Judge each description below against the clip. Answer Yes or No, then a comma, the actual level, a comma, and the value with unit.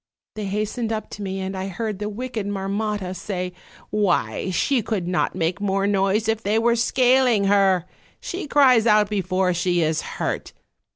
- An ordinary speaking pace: Yes, average, 170 wpm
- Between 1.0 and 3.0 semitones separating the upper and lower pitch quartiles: Yes, average, 2.7 semitones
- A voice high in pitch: Yes, high, 205 Hz